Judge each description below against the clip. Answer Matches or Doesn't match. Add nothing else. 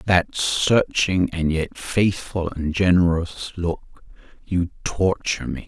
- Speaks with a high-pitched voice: Doesn't match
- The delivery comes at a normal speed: Doesn't match